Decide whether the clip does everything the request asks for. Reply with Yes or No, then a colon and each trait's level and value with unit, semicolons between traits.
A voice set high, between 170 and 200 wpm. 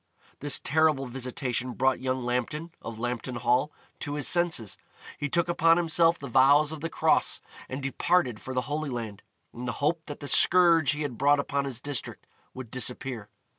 No: low, 135 Hz; average, 180 wpm